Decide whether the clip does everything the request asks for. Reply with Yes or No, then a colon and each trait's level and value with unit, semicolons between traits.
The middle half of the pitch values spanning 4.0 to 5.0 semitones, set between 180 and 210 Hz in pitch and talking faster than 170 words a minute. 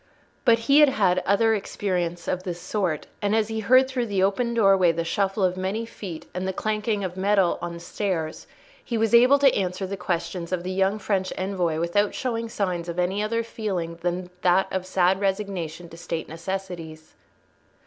No: average, 3.2 semitones; high, 190 Hz; average, 190 wpm